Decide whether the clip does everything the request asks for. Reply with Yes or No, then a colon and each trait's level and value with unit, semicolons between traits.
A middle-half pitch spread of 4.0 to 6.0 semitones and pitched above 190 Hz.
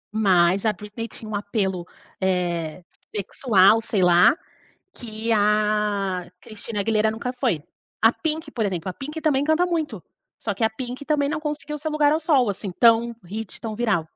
Yes: wide, 5.5 semitones; high, 220 Hz